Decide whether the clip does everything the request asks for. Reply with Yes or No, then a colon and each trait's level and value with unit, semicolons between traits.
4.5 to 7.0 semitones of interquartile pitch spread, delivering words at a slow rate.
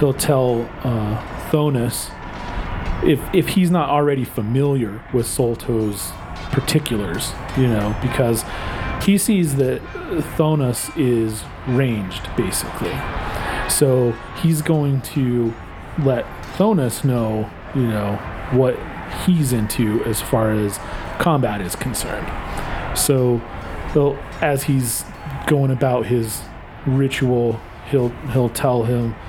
No: average, 4.0 semitones; slow, 110 wpm